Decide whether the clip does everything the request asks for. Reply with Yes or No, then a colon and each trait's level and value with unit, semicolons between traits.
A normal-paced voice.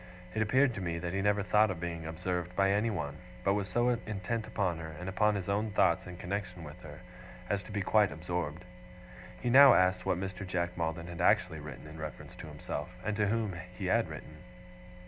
No: fast, 210 wpm